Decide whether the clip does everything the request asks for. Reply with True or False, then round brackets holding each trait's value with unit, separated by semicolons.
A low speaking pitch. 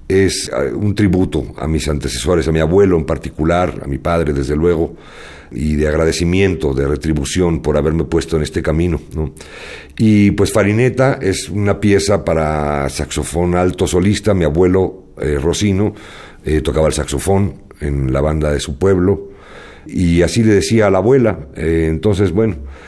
True (85 Hz)